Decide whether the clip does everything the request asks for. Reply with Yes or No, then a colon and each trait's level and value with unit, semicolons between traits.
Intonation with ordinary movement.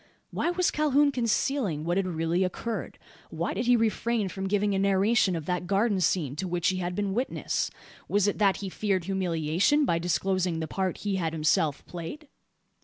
Yes: average, 3.9 semitones